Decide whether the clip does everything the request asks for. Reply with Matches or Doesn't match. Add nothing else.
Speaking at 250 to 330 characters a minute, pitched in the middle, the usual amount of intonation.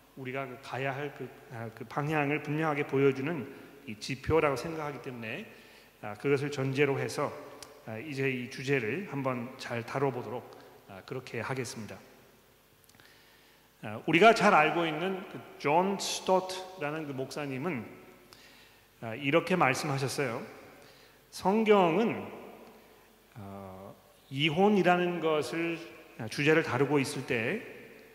Doesn't match